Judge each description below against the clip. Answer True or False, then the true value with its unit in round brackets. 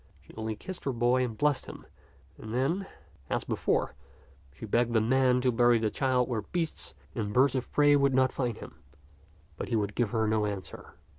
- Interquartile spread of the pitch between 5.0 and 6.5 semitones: False (3.2 semitones)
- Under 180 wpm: False (200 wpm)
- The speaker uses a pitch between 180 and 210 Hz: False (125 Hz)